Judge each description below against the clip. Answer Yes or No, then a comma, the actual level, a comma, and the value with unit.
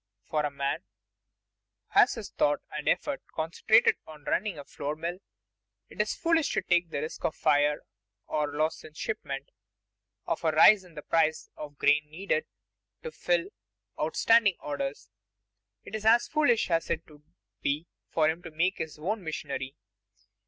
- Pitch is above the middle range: No, medium, 155 Hz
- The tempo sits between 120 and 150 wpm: No, average, 165 wpm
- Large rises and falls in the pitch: No, average, 3.9 semitones